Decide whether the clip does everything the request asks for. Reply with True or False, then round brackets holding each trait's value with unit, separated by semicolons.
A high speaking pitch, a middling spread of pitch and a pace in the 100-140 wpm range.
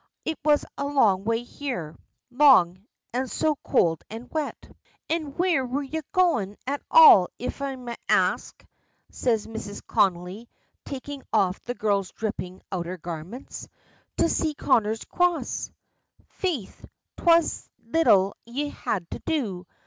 False (240 Hz; 6.9 semitones; 135 wpm)